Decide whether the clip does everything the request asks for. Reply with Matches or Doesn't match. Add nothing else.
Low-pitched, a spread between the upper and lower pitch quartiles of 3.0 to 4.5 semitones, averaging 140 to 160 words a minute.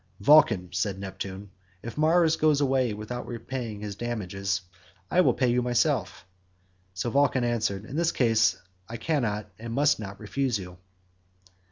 Doesn't match